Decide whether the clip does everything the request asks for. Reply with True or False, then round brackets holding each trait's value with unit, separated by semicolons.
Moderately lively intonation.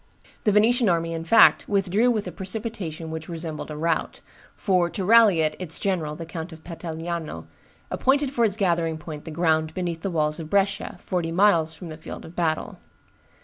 True (3.7 semitones)